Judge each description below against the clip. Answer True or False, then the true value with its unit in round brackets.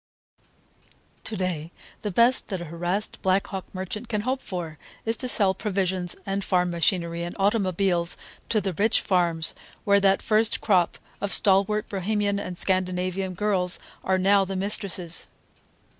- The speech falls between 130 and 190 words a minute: True (150 wpm)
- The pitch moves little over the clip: True (2.3 semitones)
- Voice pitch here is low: False (190 Hz)